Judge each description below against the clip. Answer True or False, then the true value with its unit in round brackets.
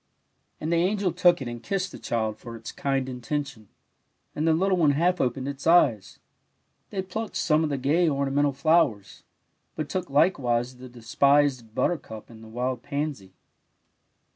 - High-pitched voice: False (140 Hz)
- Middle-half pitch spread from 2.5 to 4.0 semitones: False (5.4 semitones)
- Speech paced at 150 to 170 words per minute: True (165 wpm)